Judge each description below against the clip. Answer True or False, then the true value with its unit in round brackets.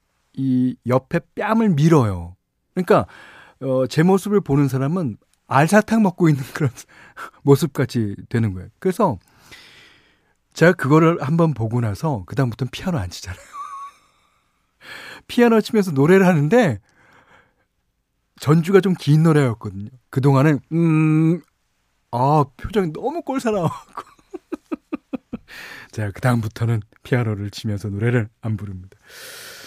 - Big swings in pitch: True (8.7 semitones)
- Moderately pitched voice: True (145 Hz)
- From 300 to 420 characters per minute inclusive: False (265 characters per minute)